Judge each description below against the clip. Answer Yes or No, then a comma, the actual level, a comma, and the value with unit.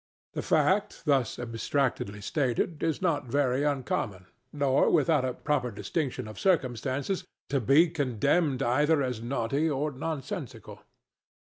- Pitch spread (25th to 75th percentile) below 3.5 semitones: No, average, 3.8 semitones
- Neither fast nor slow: No, slow, 125 wpm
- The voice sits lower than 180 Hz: Yes, medium, 140 Hz